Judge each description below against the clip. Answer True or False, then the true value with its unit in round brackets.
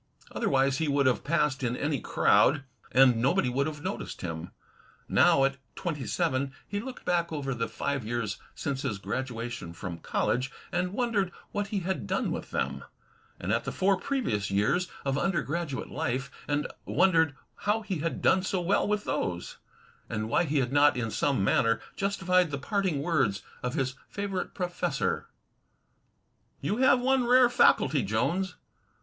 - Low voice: False (145 Hz)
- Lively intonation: True (6.8 semitones)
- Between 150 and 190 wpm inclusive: True (165 wpm)